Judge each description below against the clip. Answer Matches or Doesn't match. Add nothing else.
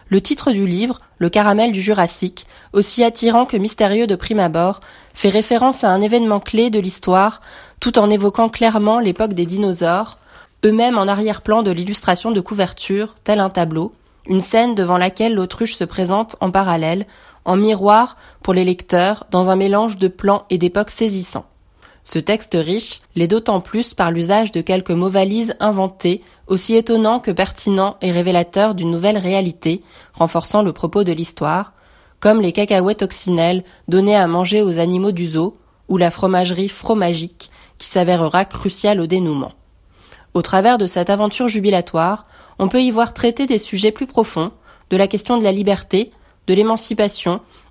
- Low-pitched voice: Doesn't match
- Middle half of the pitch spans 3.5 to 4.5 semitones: Doesn't match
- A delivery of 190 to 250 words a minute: Doesn't match